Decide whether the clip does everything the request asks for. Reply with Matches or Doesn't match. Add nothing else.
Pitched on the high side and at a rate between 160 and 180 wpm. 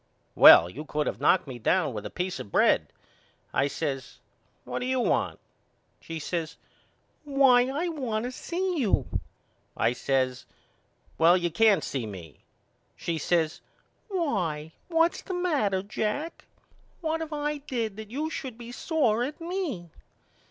Doesn't match